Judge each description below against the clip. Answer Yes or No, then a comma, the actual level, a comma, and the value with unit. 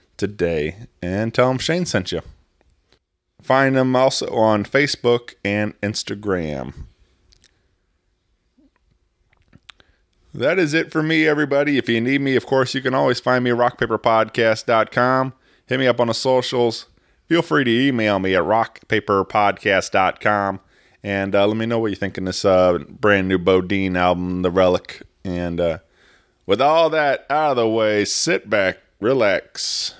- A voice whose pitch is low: Yes, low, 110 Hz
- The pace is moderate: Yes, average, 150 wpm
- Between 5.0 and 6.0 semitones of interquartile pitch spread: Yes, wide, 5.6 semitones